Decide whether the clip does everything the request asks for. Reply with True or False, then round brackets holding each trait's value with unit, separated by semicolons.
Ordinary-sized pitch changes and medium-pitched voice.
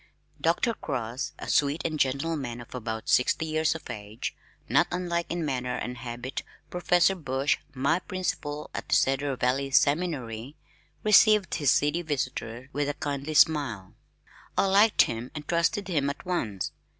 True (5.0 semitones; 145 Hz)